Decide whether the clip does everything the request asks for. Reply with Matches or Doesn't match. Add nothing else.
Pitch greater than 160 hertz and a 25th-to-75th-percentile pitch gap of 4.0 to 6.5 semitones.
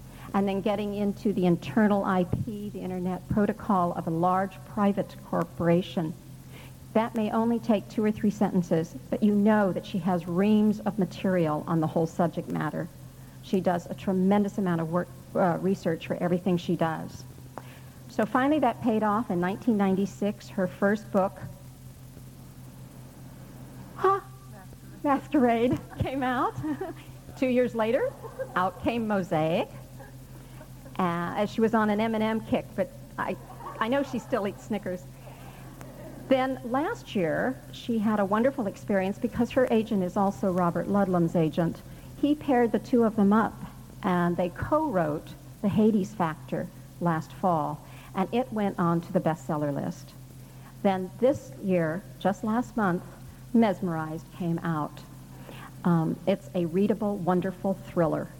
Matches